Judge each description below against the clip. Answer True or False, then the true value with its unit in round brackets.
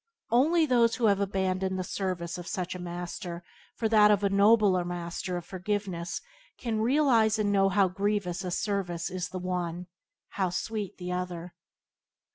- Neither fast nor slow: True (165 wpm)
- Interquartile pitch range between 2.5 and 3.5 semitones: True (2.9 semitones)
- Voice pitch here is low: False (190 Hz)